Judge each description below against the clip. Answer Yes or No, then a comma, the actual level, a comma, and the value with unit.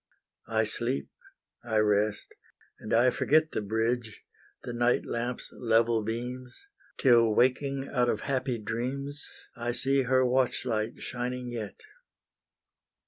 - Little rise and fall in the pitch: Yes, narrow, 2.2 semitones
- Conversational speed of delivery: No, slow, 125 wpm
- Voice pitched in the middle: No, low, 120 Hz